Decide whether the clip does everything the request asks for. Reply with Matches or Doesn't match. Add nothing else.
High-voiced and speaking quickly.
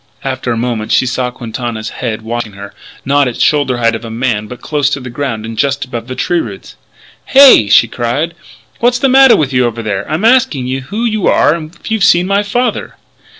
Doesn't match